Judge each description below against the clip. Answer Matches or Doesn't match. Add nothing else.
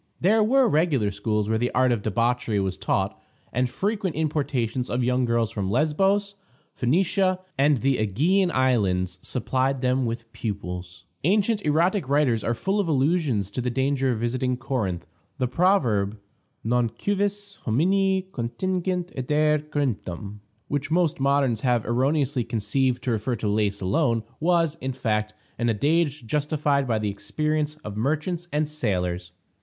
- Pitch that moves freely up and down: Matches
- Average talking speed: Matches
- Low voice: Matches